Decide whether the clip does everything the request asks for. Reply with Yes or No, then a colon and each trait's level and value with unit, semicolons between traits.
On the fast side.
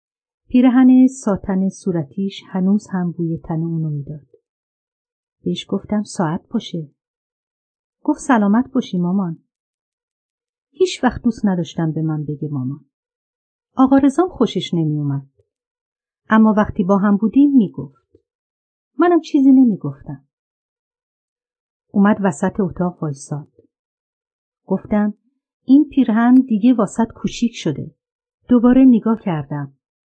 No: average, 110 wpm